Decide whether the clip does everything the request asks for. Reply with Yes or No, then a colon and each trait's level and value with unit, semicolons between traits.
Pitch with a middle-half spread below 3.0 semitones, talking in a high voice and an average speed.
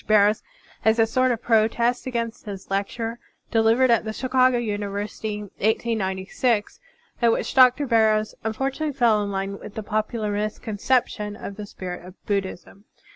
Yes: narrow, 2.5 semitones; high, 220 Hz; average, 150 wpm